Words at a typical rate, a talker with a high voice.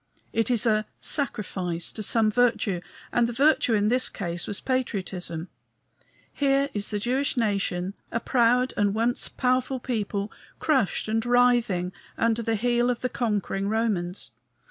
Yes: average, 145 wpm; high, 225 Hz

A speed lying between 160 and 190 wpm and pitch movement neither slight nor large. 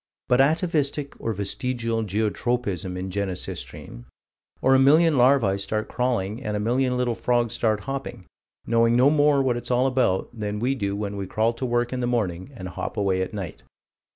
Yes: average, 180 wpm; average, 4.1 semitones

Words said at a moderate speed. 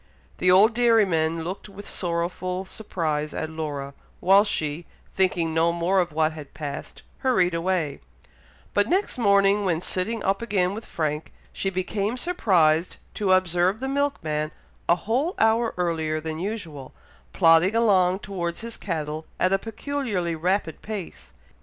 Yes: average, 145 wpm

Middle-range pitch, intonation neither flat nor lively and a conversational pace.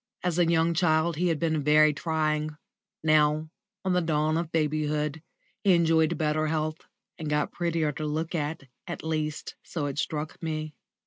No: medium, 155 Hz; narrow, 1.3 semitones; average, 170 wpm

